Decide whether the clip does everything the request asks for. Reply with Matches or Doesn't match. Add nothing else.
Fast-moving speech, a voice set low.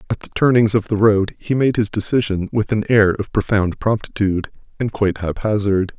Doesn't match